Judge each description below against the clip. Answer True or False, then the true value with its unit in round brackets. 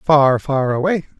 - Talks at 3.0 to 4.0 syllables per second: True (3.9 syllables/s)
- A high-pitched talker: False (145 Hz)